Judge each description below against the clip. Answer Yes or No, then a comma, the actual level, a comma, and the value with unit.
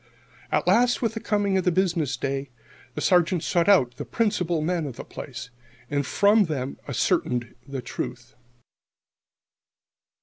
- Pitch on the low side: No, medium, 170 Hz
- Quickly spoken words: No, average, 145 wpm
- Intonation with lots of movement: Yes, wide, 6.7 semitones